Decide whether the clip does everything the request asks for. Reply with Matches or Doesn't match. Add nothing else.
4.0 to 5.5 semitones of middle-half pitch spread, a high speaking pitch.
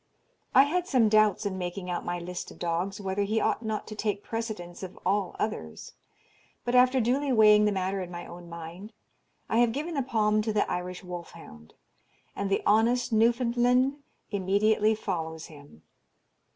Matches